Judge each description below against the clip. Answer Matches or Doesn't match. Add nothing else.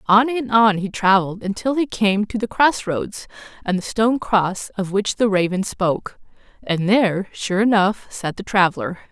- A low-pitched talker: Doesn't match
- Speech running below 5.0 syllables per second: Matches